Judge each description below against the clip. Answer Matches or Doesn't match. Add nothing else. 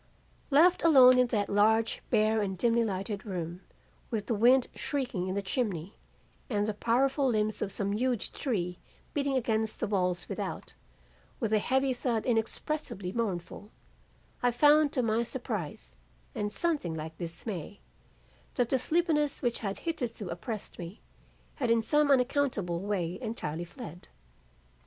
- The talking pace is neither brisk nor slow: Matches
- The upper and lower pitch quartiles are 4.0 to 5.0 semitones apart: Matches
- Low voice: Doesn't match